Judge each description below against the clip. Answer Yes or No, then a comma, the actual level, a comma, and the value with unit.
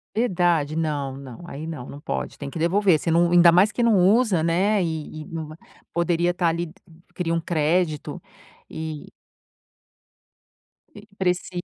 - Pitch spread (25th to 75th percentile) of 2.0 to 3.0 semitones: Yes, narrow, 2.4 semitones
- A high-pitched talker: No, medium, 170 Hz